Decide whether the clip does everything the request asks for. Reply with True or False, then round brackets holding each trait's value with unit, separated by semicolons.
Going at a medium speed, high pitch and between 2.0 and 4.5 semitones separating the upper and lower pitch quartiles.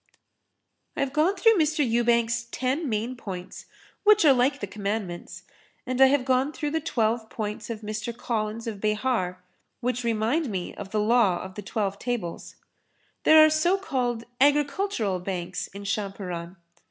False (160 wpm; 235 Hz; 5.0 semitones)